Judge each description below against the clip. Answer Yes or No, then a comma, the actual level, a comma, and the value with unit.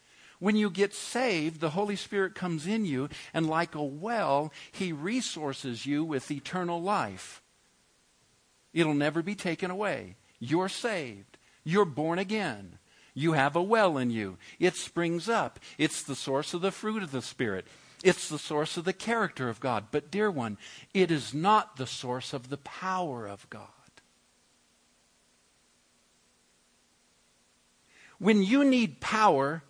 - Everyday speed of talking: Yes, average, 150 wpm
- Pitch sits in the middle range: Yes, medium, 160 Hz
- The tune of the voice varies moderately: No, wide, 6.2 semitones